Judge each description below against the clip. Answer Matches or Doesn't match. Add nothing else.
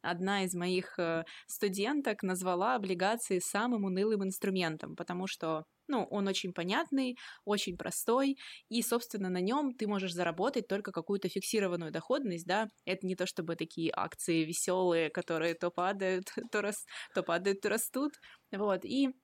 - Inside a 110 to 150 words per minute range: Matches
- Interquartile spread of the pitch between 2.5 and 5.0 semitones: Matches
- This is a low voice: Doesn't match